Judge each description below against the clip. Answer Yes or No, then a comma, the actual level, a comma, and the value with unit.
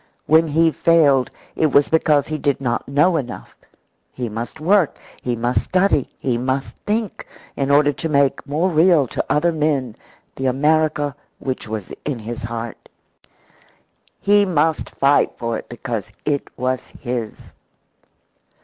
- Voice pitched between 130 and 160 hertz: Yes, medium, 140 Hz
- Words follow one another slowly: No, average, 145 wpm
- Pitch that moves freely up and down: No, average, 4.1 semitones